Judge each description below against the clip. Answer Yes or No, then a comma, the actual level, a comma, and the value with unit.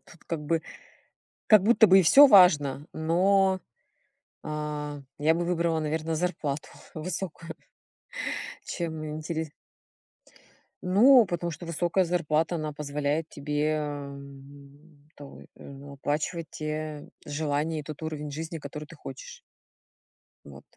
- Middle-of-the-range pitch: Yes, medium, 155 Hz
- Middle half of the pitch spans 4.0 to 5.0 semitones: No, narrow, 2.6 semitones